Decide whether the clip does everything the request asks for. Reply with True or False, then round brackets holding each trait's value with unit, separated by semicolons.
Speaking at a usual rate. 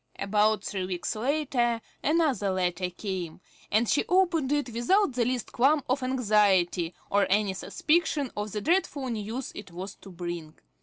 True (155 wpm)